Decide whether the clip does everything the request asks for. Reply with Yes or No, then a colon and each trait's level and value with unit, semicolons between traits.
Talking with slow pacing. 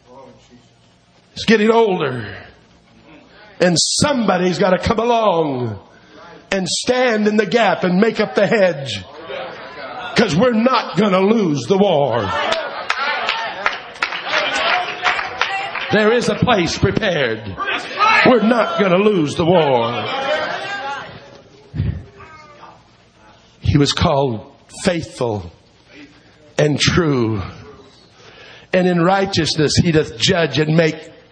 Yes: slow, 100 wpm